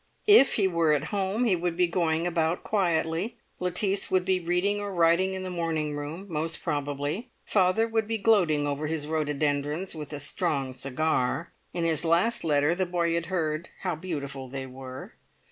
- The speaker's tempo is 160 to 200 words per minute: Yes, average, 180 wpm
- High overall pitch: No, medium, 165 Hz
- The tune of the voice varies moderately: Yes, average, 3.9 semitones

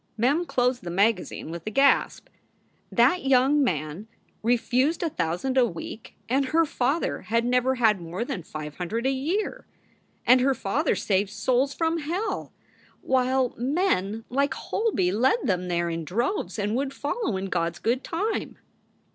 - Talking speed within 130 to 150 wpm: No, average, 160 wpm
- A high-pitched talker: Yes, high, 245 Hz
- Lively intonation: Yes, wide, 6.0 semitones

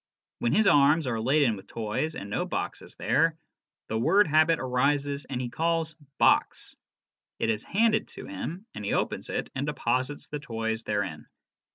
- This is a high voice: No, medium, 140 Hz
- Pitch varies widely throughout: Yes, wide, 5.7 semitones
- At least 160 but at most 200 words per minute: Yes, average, 185 wpm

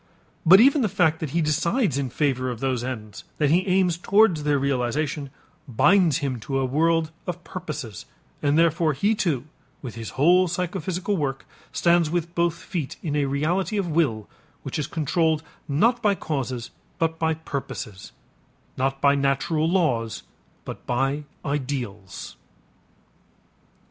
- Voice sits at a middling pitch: Yes, medium, 150 Hz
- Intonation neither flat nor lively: Yes, average, 4.2 semitones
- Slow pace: No, average, 150 wpm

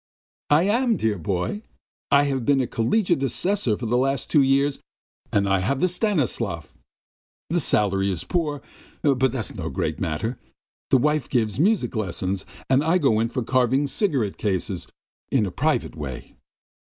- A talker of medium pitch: No, low, 130 Hz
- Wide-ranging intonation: Yes, wide, 6.1 semitones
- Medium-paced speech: Yes, average, 165 wpm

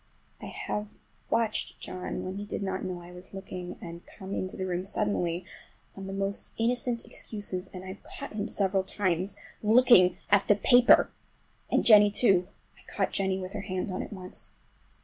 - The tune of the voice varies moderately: No, narrow, 2.1 semitones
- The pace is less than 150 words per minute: No, average, 180 wpm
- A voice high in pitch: Yes, high, 195 Hz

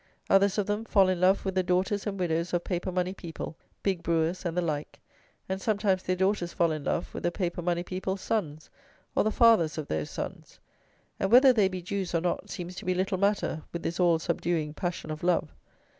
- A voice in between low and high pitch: Yes, medium, 180 Hz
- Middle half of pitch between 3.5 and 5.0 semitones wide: No, narrow, 2.4 semitones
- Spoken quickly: Yes, fast, 220 wpm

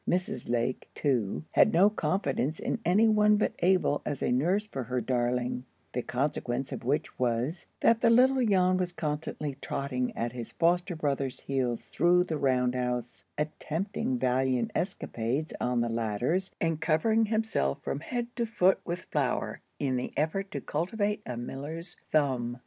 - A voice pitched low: No, medium, 150 Hz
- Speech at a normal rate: Yes, average, 160 wpm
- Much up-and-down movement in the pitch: Yes, wide, 6.7 semitones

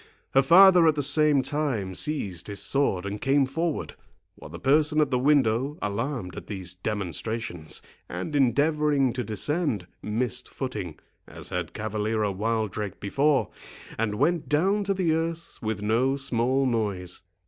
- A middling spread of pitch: No, wide, 6.1 semitones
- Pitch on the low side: Yes, low, 130 Hz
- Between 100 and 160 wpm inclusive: Yes, average, 150 wpm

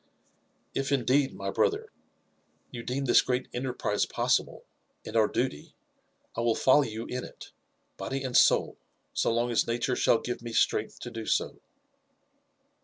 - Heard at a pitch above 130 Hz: No, low, 125 Hz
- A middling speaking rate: Yes, average, 155 wpm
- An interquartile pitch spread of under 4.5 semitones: Yes, narrow, 2.4 semitones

